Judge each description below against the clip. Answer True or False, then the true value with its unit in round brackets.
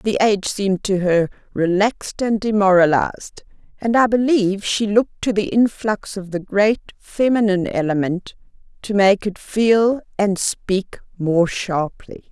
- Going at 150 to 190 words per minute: False (140 wpm)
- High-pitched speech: True (200 Hz)